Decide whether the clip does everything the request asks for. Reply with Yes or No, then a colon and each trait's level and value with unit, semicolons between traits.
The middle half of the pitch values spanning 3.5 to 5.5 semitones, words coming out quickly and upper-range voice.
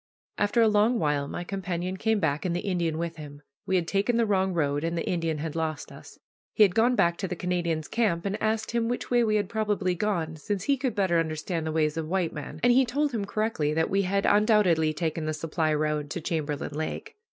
No: average, 4.8 semitones; fast, 235 wpm; medium, 175 Hz